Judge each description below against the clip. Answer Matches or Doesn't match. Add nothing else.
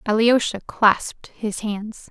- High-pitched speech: Matches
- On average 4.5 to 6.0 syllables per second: Doesn't match